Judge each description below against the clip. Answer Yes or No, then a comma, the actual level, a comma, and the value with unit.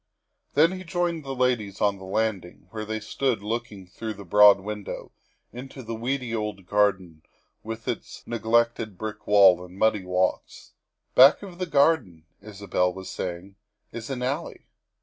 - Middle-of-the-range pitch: No, low, 110 Hz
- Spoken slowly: No, average, 165 wpm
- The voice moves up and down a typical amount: Yes, average, 4.4 semitones